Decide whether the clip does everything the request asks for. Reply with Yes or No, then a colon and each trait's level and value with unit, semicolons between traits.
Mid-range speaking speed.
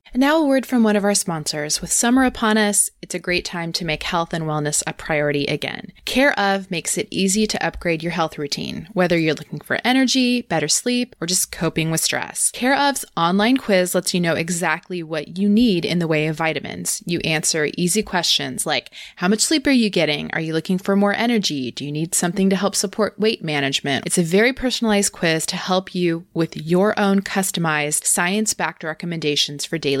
No: fast, 210 wpm